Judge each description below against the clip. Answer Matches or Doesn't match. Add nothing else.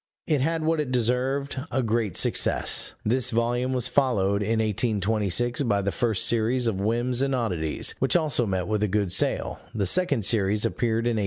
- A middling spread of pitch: Matches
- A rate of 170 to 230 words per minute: Matches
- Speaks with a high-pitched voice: Doesn't match